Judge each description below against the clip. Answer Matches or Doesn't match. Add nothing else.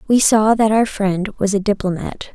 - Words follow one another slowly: Doesn't match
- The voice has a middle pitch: Doesn't match